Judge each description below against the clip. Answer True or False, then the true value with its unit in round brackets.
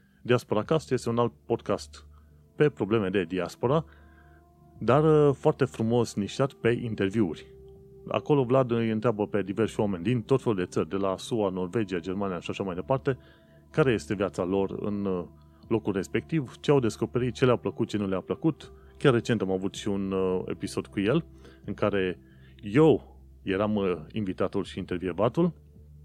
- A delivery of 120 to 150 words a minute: False (160 wpm)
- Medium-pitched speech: False (100 Hz)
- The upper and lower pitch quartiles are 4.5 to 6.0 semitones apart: True (5.0 semitones)